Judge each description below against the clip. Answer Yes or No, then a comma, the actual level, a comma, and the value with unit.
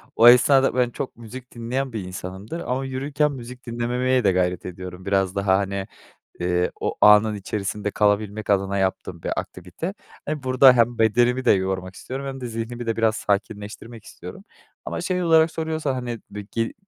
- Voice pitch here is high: No, low, 115 Hz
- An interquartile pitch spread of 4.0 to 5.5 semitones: Yes, average, 4.6 semitones